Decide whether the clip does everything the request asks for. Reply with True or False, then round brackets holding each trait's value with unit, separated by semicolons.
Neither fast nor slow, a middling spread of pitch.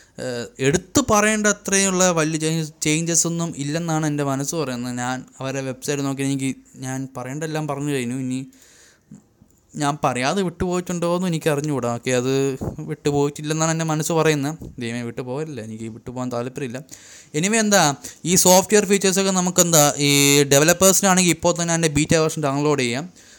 False (135 wpm; 4.1 semitones)